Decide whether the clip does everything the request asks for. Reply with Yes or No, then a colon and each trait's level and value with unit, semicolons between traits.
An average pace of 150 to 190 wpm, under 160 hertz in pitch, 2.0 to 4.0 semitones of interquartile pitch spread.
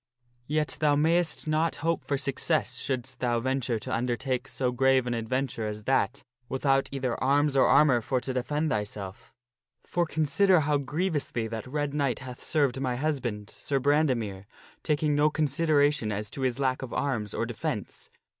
Yes: average, 165 wpm; low, 135 Hz; average, 3.5 semitones